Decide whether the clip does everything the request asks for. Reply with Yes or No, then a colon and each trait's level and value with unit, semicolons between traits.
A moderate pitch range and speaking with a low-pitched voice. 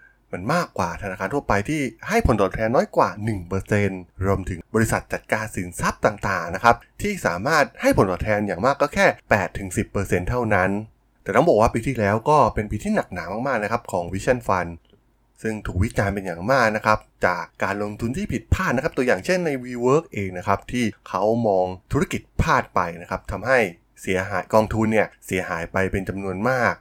Yes: average, 3.5 semitones; low, 105 Hz